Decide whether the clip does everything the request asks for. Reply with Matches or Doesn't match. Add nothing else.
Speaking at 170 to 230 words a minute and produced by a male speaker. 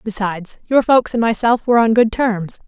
Doesn't match